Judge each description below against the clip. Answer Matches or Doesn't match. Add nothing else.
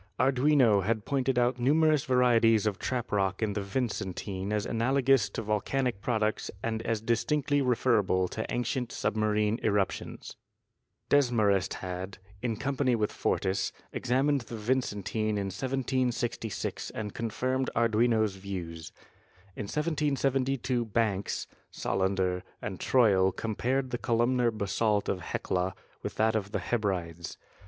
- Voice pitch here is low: Matches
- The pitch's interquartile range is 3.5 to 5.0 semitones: Matches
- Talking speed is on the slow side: Matches